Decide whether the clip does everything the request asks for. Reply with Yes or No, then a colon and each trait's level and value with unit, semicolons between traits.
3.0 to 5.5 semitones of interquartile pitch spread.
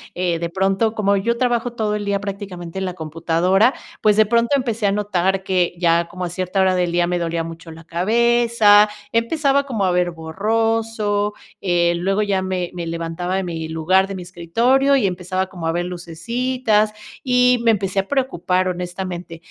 Yes: average, 4.0 semitones